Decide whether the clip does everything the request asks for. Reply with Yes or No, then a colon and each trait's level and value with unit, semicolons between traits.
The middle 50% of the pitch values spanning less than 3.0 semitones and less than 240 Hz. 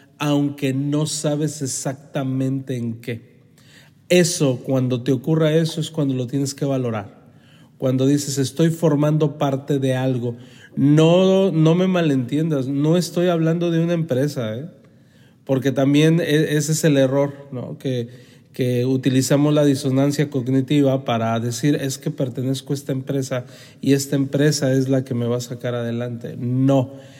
Yes: narrow, 2.5 semitones; medium, 140 Hz